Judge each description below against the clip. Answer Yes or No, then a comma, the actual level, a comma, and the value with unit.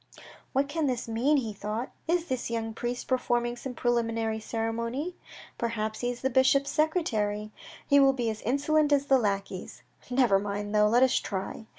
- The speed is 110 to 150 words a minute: No, average, 175 wpm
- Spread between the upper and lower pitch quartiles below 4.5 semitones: Yes, average, 3.6 semitones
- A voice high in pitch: Yes, high, 240 Hz